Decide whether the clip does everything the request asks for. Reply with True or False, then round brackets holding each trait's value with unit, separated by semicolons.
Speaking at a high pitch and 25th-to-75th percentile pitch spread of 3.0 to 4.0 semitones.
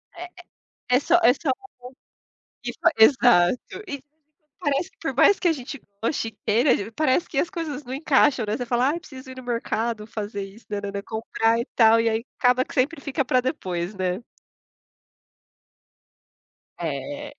False (250 Hz; 4.4 semitones)